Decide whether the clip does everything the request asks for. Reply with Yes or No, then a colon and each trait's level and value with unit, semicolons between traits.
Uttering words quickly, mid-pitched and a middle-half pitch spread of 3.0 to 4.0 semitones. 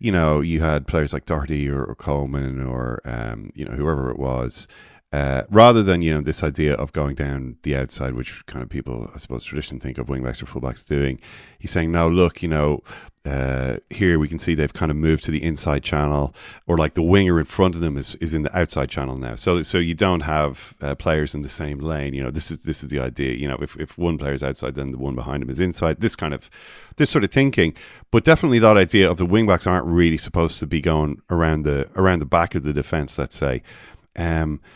No: fast, 245 wpm; very low, 75 Hz; average, 3.6 semitones